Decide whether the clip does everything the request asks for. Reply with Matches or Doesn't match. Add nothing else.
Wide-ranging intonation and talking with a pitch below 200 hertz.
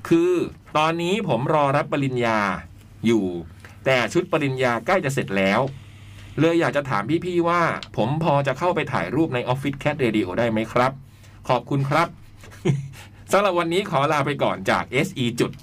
Matches